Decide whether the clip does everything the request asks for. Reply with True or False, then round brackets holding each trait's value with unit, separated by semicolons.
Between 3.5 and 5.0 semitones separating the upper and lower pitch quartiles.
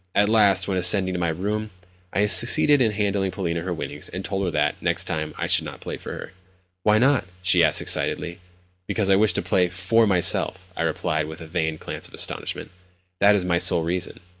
False (3.1 semitones)